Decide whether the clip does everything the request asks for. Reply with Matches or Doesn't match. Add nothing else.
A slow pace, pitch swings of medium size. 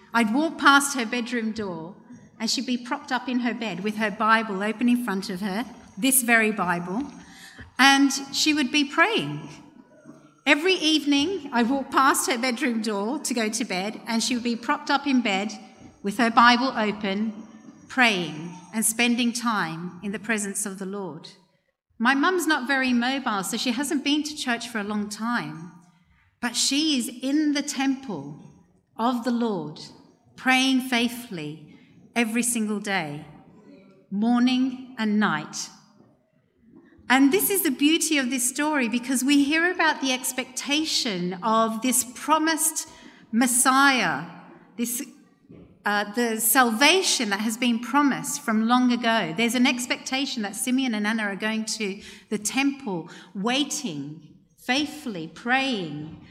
Doesn't match